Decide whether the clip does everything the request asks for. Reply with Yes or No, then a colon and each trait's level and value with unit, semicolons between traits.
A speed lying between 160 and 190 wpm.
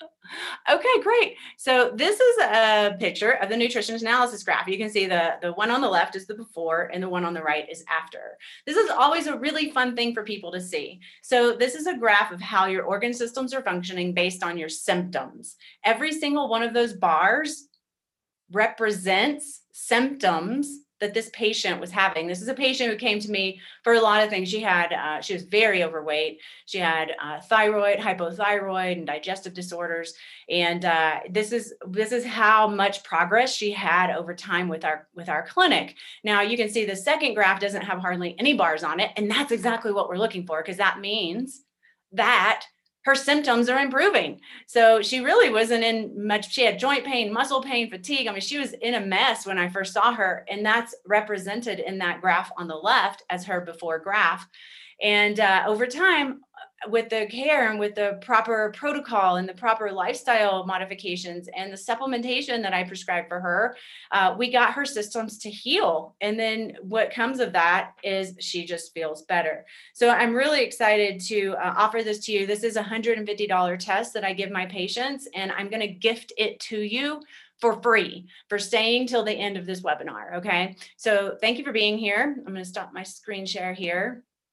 No: average, 200 wpm